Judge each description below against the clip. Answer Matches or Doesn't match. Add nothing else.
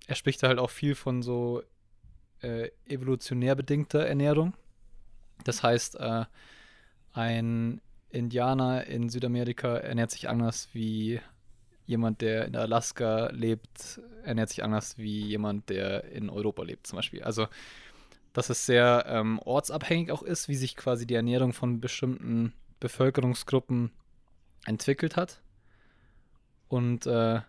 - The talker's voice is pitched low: Matches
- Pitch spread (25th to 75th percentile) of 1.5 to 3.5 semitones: Matches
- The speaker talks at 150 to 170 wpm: Doesn't match